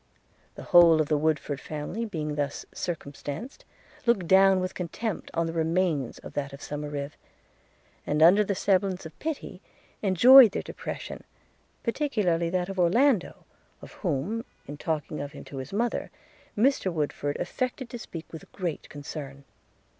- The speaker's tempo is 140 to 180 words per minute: Yes, average, 150 wpm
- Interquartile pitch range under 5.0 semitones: No, wide, 5.4 semitones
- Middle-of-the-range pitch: Yes, medium, 170 Hz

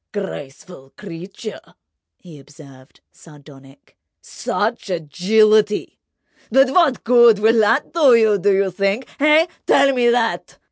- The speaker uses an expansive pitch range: Yes, wide, 6.3 semitones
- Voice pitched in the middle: No, high, 210 Hz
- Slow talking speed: Yes, slow, 120 wpm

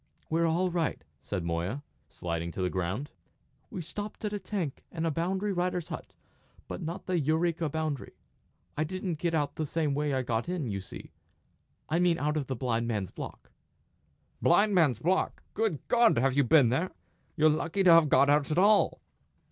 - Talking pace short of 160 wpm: No, average, 190 wpm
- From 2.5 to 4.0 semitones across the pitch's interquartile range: No, average, 5.1 semitones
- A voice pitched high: No, medium, 155 Hz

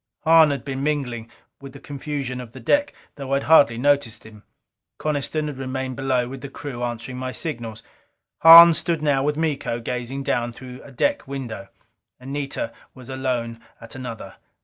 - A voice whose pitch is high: No, low, 135 Hz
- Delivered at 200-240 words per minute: No, average, 170 wpm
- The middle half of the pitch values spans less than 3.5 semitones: Yes, average, 2.9 semitones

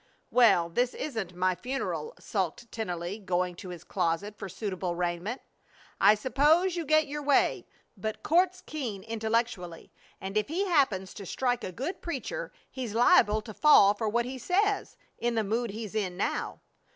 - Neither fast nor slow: Yes, average, 165 wpm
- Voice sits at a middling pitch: No, high, 220 Hz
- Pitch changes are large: Yes, wide, 6.2 semitones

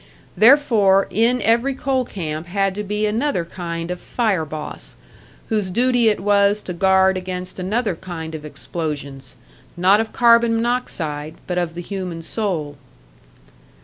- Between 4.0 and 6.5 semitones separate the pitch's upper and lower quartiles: Yes, average, 4.9 semitones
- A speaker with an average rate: Yes, average, 145 wpm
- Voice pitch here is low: No, high, 190 Hz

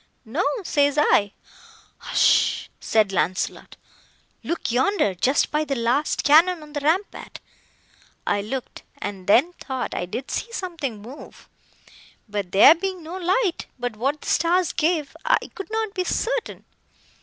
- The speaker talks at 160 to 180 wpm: No, slow, 135 wpm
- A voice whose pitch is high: Yes, very high, 295 Hz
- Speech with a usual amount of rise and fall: No, wide, 7.5 semitones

